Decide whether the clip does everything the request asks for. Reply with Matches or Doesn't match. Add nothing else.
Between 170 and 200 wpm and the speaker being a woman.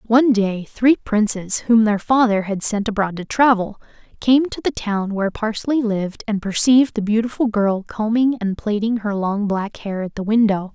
Matches